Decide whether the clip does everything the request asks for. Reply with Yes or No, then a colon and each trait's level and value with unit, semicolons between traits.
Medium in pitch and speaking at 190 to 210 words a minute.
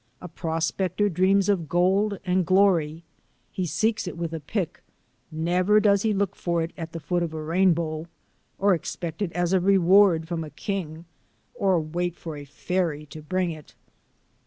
No: medium, 175 Hz; average, 175 wpm